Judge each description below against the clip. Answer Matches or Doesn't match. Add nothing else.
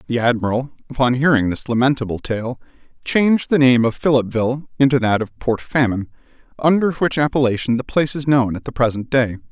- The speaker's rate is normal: Matches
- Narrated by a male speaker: Matches